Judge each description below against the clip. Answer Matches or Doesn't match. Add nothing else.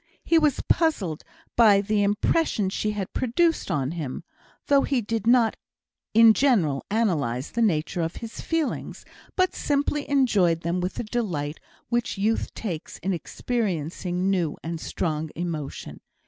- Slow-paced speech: Doesn't match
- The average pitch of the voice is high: Matches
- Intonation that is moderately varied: Doesn't match